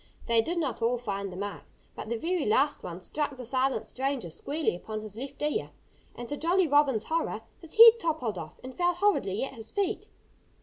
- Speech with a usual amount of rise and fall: No, wide, 6.8 semitones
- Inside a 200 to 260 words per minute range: Yes, fast, 205 wpm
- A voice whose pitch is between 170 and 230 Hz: No, very high, 265 Hz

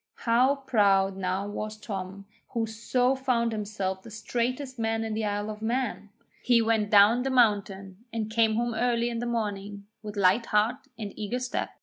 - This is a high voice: Yes, high, 220 Hz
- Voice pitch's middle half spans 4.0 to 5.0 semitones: No, narrow, 2.6 semitones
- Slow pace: No, average, 180 wpm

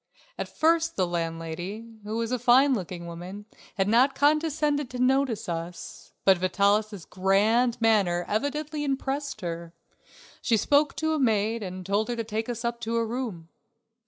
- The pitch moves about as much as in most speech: No, wide, 6.0 semitones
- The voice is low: No, high, 225 Hz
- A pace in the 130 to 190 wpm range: Yes, average, 160 wpm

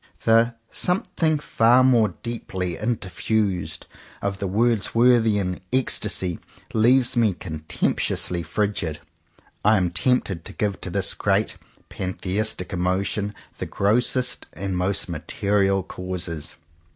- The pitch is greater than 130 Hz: No, low, 100 Hz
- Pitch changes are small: No, average, 4.0 semitones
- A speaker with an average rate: No, slow, 110 wpm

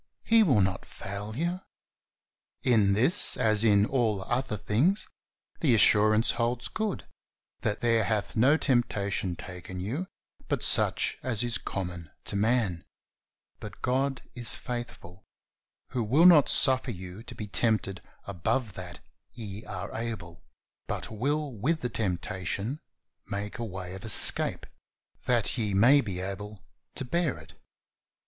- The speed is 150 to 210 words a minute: No, average, 140 wpm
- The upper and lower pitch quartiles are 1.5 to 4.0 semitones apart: No, average, 4.4 semitones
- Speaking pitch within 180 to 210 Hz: No, low, 110 Hz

